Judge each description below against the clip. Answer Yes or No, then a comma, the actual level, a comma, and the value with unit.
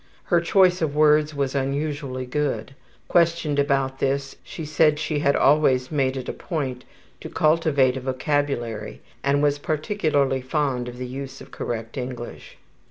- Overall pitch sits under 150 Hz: Yes, medium, 140 Hz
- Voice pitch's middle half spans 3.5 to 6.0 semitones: No, average, 2.7 semitones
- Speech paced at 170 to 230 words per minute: No, average, 155 wpm